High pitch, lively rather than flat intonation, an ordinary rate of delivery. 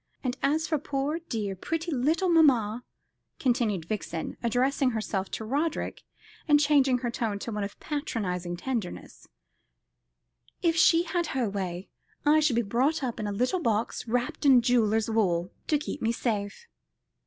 Yes: high, 245 Hz; wide, 5.8 semitones; average, 155 wpm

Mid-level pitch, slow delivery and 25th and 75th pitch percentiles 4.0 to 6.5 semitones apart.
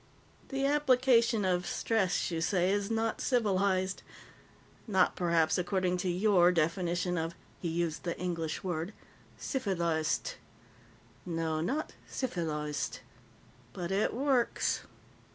Yes: medium, 180 Hz; slow, 110 wpm; average, 4.4 semitones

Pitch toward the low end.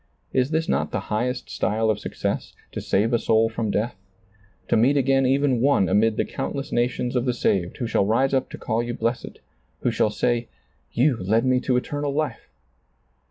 Yes: low, 120 Hz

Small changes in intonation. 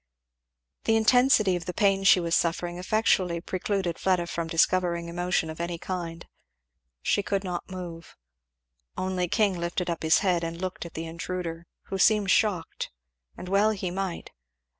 Yes: narrow, 2.3 semitones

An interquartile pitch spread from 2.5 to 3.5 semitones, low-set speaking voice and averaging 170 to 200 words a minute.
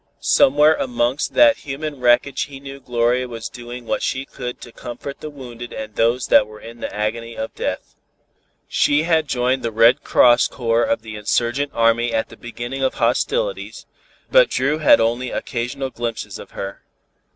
Yes: average, 2.9 semitones; low, 125 Hz; average, 175 wpm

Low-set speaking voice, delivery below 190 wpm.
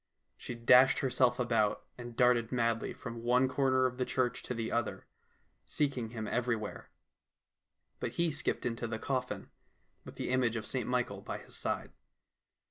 Yes: low, 125 Hz; average, 160 wpm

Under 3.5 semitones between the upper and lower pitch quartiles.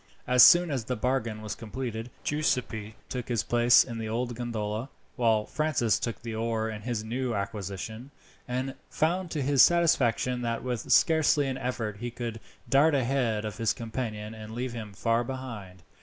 Yes: average, 2.8 semitones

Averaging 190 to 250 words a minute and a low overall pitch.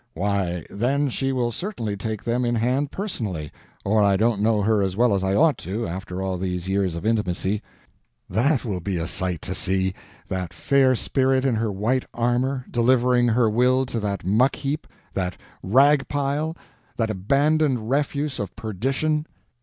No: average, 170 wpm; low, 115 Hz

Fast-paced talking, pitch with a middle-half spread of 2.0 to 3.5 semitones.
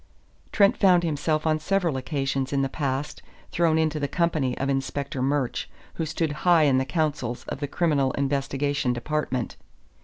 No: average, 165 wpm; average, 2.9 semitones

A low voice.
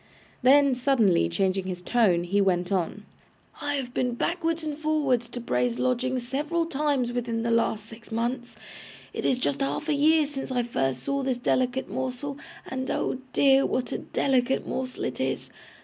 No: very high, 250 Hz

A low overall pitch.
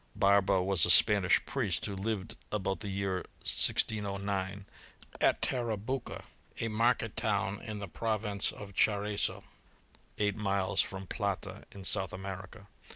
Yes: low, 100 Hz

